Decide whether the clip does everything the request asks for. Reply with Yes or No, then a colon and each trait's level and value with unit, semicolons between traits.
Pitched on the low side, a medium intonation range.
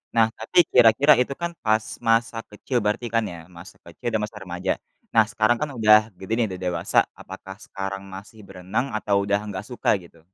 Yes: low, 105 Hz; average, 3.1 semitones